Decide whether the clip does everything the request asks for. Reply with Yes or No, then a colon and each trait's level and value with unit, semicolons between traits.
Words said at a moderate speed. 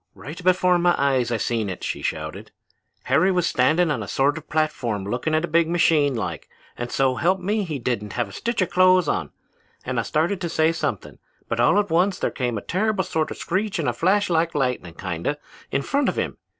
No: fast, 225 wpm